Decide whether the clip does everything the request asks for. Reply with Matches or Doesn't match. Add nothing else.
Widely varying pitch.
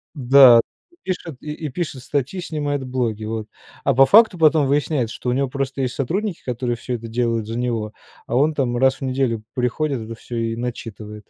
Doesn't match